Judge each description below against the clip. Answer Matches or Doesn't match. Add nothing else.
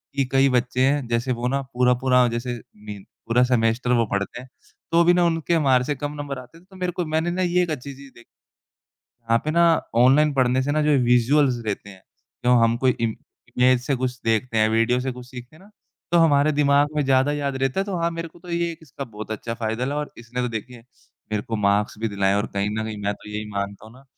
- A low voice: Matches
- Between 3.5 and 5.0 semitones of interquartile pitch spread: Matches